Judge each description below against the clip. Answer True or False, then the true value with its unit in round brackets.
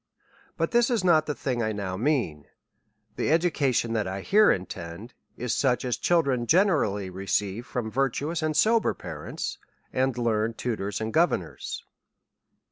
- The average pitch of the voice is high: False (120 Hz)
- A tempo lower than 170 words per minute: True (155 wpm)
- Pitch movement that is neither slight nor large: False (7.2 semitones)